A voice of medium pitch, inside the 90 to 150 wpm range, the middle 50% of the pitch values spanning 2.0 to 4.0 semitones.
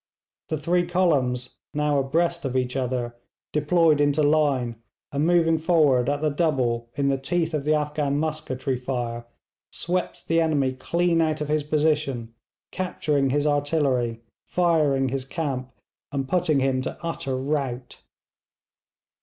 Yes: medium, 145 Hz; average, 140 wpm; average, 3.4 semitones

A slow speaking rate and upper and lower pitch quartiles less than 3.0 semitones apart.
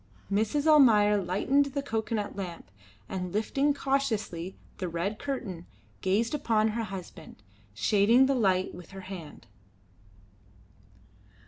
No: slow, 115 wpm; wide, 5.6 semitones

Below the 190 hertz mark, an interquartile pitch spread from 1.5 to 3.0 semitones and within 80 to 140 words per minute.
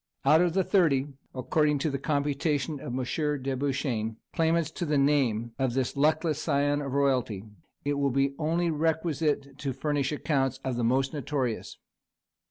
No: medium, 140 Hz; narrow, 2.5 semitones; average, 165 wpm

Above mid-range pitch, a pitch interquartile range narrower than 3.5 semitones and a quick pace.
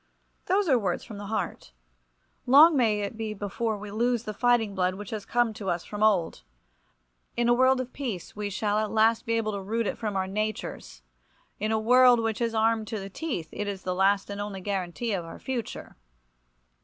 Yes: high, 215 Hz; average, 2.8 semitones; fast, 215 wpm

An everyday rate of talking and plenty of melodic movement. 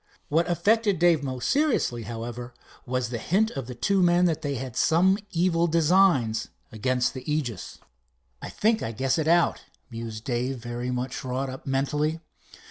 Yes: average, 165 wpm; wide, 5.9 semitones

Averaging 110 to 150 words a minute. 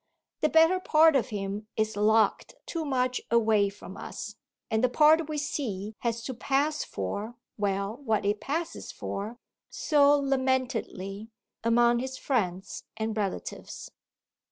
Yes: slow, 135 wpm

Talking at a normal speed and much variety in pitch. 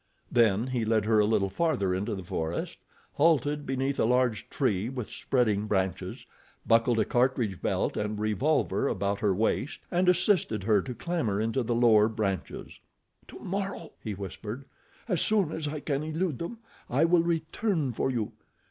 Yes: average, 165 wpm; wide, 6.4 semitones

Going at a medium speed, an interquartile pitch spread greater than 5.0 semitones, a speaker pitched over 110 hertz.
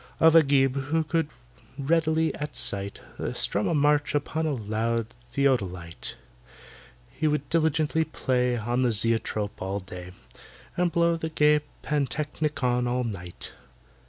No: slow, 130 wpm; wide, 5.4 semitones; medium, 140 Hz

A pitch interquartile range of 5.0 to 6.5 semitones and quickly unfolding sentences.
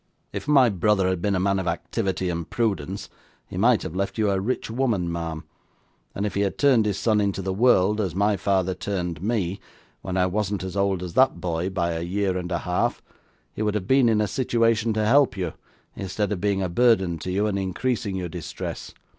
No: average, 2.7 semitones; fast, 220 wpm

